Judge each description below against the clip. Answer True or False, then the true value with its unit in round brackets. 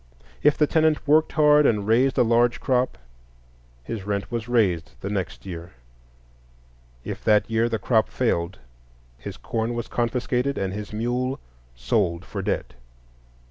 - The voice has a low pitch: True (115 Hz)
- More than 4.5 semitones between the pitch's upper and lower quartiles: False (4.0 semitones)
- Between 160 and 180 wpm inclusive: False (145 wpm)